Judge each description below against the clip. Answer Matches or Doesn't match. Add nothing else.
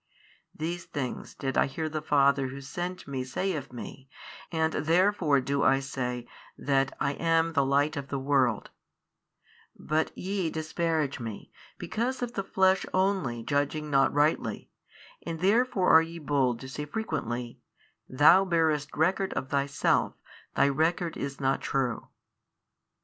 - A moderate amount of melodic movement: Matches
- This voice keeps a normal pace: Matches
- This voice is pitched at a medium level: Matches